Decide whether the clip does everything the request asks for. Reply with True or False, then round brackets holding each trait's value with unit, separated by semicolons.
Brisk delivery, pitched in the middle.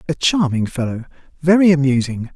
False (125 wpm; 145 Hz)